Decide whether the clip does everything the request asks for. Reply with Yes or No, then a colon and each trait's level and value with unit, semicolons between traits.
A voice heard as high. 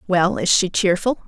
Yes: high, 195 Hz